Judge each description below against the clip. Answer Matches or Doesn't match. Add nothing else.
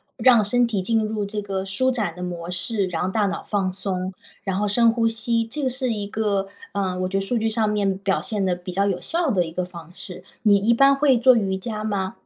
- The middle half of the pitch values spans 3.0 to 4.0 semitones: Matches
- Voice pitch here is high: Matches